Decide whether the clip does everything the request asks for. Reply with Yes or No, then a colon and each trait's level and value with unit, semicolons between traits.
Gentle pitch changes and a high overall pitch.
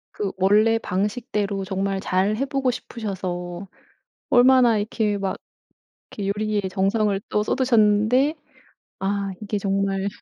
Yes: narrow, 2.3 semitones; high, 205 Hz